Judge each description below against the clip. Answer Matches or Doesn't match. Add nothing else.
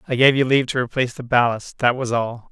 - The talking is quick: Matches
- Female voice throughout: Doesn't match